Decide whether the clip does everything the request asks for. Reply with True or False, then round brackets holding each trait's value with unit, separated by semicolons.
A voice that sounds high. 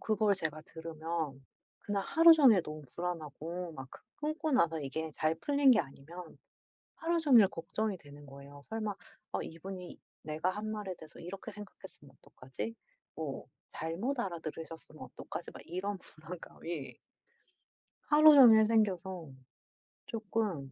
False (180 Hz)